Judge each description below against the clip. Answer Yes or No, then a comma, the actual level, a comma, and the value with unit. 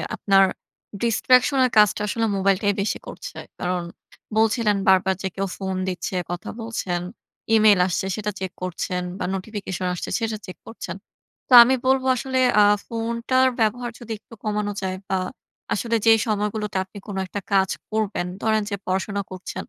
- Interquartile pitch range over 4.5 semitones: No, average, 3.0 semitones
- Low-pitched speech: No, high, 210 Hz